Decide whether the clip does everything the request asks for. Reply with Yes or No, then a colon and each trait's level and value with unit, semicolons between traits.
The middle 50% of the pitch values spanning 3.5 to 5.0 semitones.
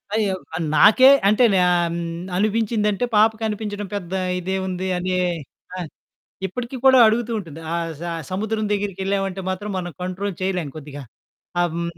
No: average, 2.9 semitones